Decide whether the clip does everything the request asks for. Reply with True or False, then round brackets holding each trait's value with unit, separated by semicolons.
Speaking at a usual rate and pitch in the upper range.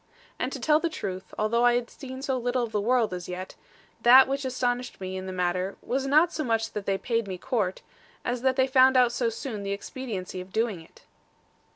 False (225 wpm; 240 Hz)